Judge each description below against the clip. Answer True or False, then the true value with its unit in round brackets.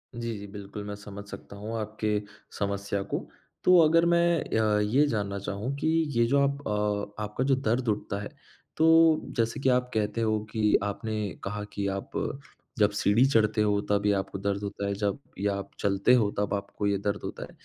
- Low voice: True (105 Hz)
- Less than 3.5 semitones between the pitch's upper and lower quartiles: True (3.1 semitones)